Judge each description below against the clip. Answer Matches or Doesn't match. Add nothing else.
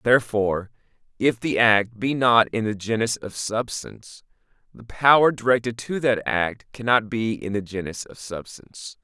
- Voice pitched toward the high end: Doesn't match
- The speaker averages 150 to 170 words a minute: Matches